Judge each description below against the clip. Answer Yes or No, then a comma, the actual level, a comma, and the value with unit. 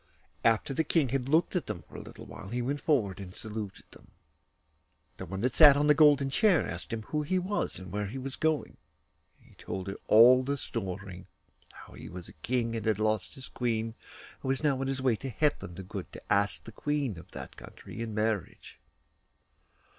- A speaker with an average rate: No, fast, 210 wpm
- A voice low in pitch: Yes, low, 120 Hz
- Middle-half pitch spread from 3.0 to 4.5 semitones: No, wide, 5.5 semitones